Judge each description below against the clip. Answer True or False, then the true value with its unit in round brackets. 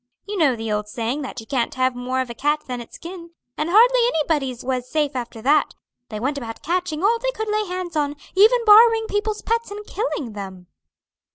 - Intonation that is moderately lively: False (8.9 semitones)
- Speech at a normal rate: False (210 wpm)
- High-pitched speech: True (300 Hz)